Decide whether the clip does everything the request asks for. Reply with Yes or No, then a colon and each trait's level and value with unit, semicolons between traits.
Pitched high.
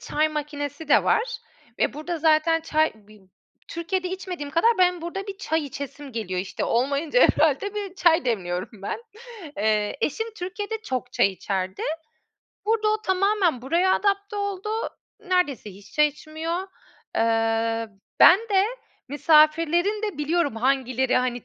Yes: very high, 310 Hz